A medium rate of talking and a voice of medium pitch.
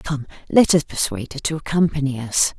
Yes: average, 185 wpm; medium, 145 Hz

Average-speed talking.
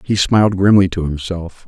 Yes: average, 180 wpm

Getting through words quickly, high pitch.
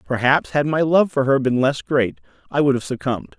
No: fast, 230 wpm; low, 135 Hz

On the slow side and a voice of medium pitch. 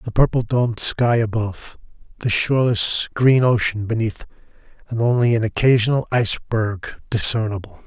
No: slow, 120 wpm; low, 115 Hz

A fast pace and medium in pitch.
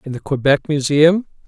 No: average, 160 wpm; medium, 150 Hz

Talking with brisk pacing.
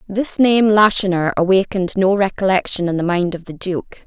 No: average, 175 wpm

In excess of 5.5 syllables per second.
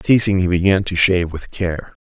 No: 5.4 syllables/s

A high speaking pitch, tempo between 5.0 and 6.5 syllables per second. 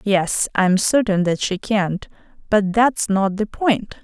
No: high, 205 Hz; 3.8 syllables/s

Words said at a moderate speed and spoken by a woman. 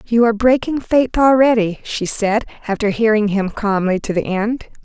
Yes: average, 175 wpm; female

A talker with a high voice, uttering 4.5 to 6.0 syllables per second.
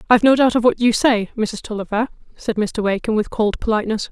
No: high, 225 Hz; 6.2 syllables/s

